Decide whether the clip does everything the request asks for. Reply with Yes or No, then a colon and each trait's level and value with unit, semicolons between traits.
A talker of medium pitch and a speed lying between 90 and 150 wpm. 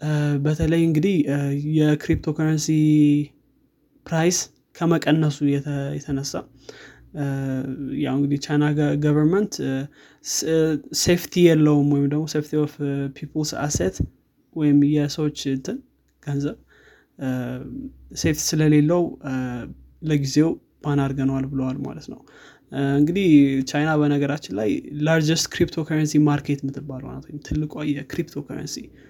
No: medium, 150 Hz; average, 80 wpm